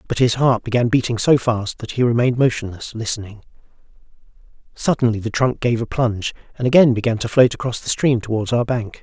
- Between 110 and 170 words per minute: No, average, 195 wpm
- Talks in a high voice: No, low, 120 Hz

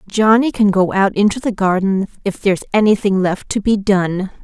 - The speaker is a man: No, female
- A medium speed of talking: Yes, average, 190 wpm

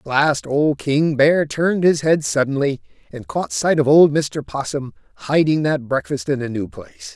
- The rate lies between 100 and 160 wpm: No, average, 195 wpm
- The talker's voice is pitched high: No, low, 135 Hz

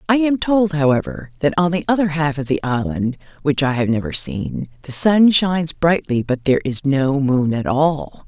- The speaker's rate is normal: Yes, average, 190 wpm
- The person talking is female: Yes, female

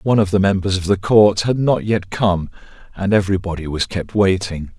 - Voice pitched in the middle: No, very low, 95 Hz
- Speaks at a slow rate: No, average, 200 wpm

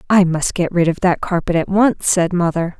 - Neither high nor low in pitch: Yes, medium, 180 Hz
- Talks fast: Yes, fast, 235 wpm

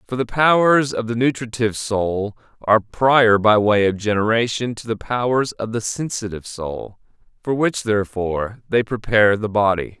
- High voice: No, low, 110 Hz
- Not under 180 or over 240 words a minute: No, average, 160 wpm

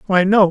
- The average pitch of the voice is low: No, high, 190 Hz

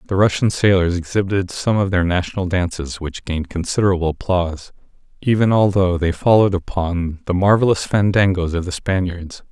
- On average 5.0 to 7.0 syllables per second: Yes, 5.6 syllables/s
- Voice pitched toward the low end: Yes, very low, 90 Hz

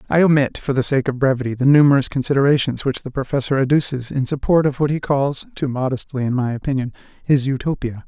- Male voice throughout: Yes, male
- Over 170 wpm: Yes, average, 200 wpm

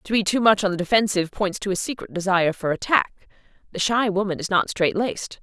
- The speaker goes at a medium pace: No, fast, 230 wpm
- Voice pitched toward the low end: No, high, 195 Hz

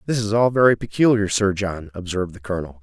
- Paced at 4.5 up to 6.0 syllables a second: No, 6.5 syllables/s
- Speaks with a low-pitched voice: Yes, low, 100 Hz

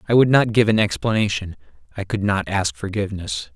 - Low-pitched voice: Yes, low, 100 Hz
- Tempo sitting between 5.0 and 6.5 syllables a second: Yes, 5.7 syllables/s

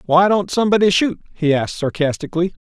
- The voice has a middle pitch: Yes, medium, 175 Hz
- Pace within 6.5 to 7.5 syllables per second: Yes, 6.7 syllables/s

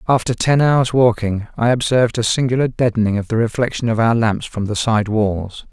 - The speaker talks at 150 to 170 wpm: No, average, 200 wpm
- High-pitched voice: No, low, 115 Hz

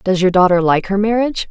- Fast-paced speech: Yes, fast, 240 wpm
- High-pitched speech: Yes, high, 195 Hz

